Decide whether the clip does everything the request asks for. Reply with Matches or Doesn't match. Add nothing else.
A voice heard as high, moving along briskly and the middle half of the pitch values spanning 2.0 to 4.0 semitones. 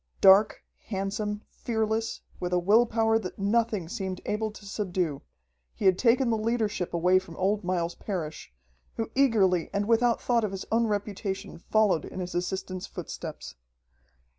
Doesn't match